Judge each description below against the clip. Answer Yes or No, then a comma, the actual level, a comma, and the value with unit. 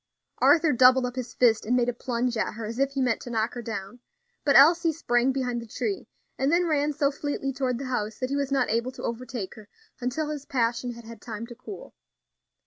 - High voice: Yes, very high, 250 Hz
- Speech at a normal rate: No, fast, 230 wpm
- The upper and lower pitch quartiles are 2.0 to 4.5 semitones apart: Yes, average, 2.9 semitones